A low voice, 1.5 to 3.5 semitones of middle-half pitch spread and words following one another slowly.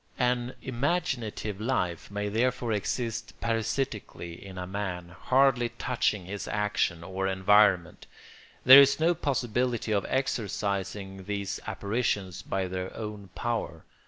No: low, 105 Hz; average, 4.3 semitones; slow, 120 wpm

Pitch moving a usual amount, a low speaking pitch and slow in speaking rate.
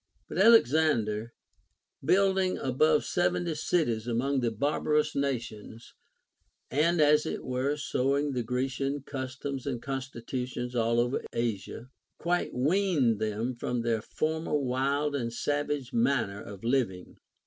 Yes: average, 3.8 semitones; low, 130 Hz; slow, 120 wpm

